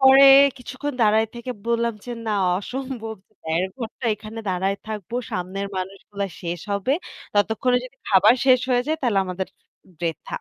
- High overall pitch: Yes, high, 220 Hz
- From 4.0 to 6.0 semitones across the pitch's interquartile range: Yes, average, 4.4 semitones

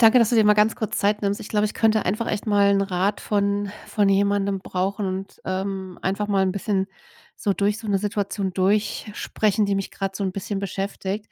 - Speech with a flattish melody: Yes, narrow, 1.4 semitones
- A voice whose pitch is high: Yes, high, 200 Hz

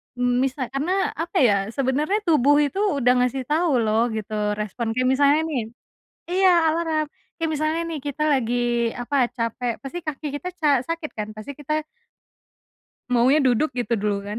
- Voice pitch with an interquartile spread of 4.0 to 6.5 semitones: Yes, average, 4.6 semitones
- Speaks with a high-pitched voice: Yes, very high, 270 Hz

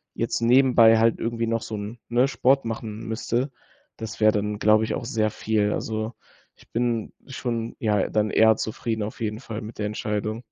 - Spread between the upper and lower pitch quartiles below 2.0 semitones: Yes, narrow, 1.5 semitones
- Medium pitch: No, low, 110 Hz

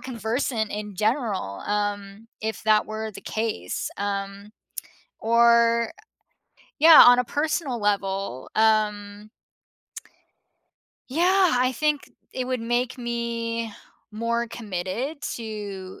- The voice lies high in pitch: Yes, high, 225 Hz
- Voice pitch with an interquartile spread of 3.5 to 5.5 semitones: No, average, 2.9 semitones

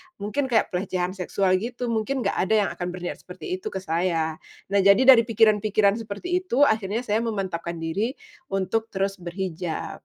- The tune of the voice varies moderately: Yes, average, 3.8 semitones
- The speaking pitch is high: Yes, high, 200 Hz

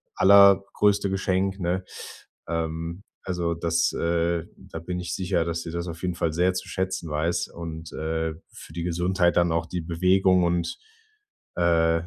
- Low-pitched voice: Yes, very low, 85 Hz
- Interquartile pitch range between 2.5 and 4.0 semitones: No, narrow, 1.9 semitones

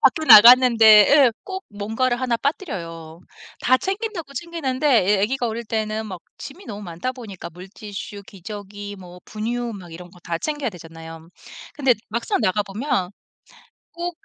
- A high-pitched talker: Yes, high, 220 Hz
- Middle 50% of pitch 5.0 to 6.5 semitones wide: Yes, wide, 5.6 semitones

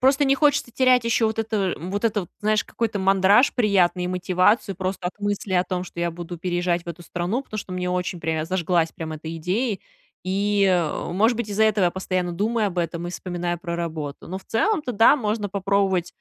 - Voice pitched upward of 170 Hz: Yes, high, 190 Hz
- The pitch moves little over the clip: No, average, 3.5 semitones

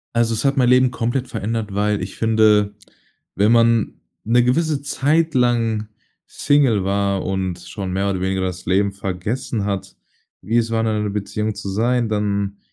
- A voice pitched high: No, low, 105 Hz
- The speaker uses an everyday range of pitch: Yes, average, 3.2 semitones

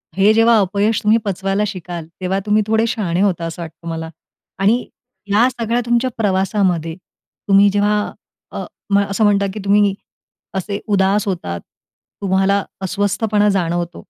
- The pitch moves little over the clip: Yes, narrow, 2.3 semitones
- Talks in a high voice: Yes, high, 200 Hz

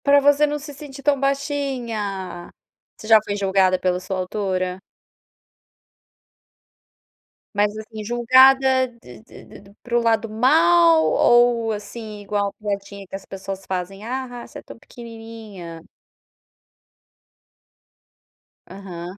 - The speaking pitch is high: Yes, high, 210 Hz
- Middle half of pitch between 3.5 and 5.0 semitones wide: Yes, average, 4.2 semitones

